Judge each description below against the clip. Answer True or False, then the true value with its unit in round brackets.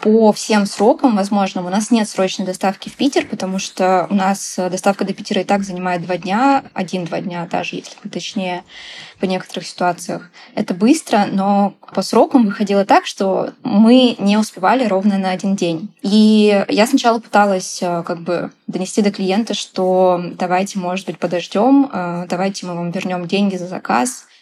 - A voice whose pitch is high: True (195 Hz)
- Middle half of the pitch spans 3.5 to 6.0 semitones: False (2.7 semitones)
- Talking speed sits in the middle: False (165 wpm)